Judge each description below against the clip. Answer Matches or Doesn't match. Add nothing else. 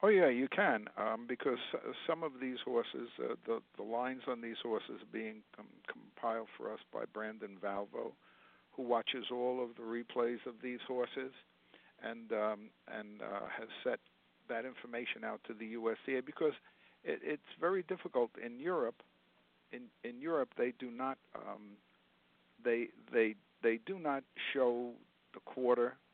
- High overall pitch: Doesn't match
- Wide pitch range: Doesn't match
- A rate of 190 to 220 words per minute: Doesn't match